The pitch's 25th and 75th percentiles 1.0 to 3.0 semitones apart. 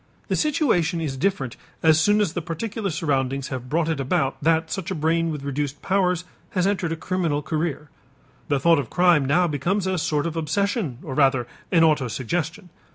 No: average, 4.1 semitones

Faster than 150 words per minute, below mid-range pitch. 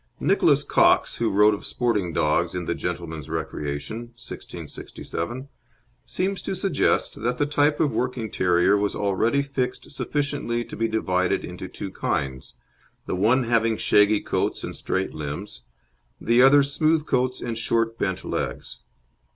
No: average, 145 wpm; low, 115 Hz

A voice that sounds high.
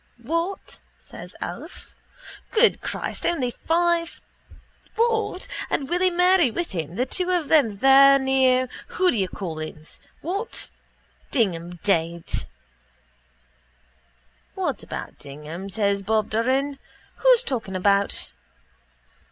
Yes: very high, 260 Hz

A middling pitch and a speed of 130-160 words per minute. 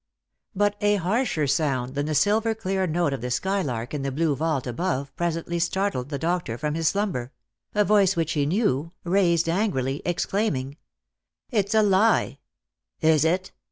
No: medium, 165 Hz; average, 175 wpm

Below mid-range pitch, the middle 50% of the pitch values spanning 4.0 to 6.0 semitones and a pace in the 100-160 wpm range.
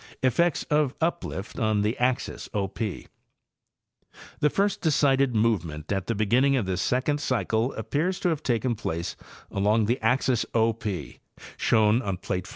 Yes: low, 115 Hz; average, 4.7 semitones; average, 155 wpm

